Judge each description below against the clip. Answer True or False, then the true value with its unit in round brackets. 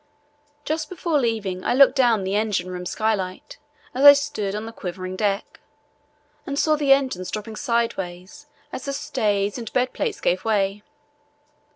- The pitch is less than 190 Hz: False (220 Hz)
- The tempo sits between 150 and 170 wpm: True (160 wpm)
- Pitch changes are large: True (6.1 semitones)